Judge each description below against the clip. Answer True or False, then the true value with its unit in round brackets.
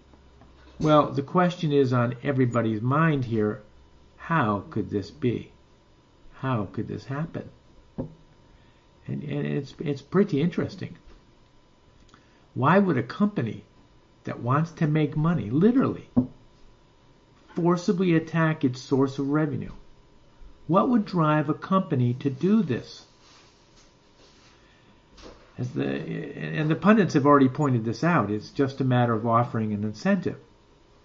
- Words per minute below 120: False (125 wpm)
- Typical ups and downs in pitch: False (5.8 semitones)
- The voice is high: False (140 Hz)